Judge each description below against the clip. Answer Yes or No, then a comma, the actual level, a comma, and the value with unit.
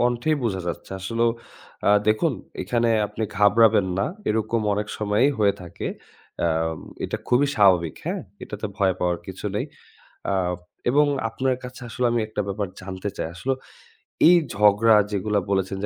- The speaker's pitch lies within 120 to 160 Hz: No, low, 105 Hz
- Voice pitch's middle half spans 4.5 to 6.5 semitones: No, average, 3.1 semitones